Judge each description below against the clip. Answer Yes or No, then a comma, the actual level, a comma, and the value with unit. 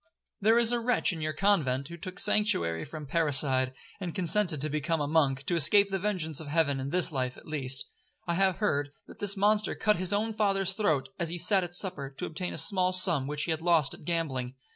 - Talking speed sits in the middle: No, fast, 230 wpm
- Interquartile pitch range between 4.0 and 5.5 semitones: Yes, average, 5.2 semitones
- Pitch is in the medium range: Yes, medium, 170 Hz